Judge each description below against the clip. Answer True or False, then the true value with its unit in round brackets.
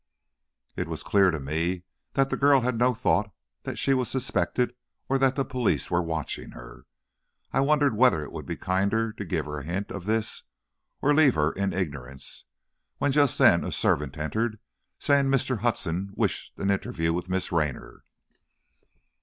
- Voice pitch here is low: True (100 Hz)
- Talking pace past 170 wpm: True (180 wpm)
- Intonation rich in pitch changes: True (7.5 semitones)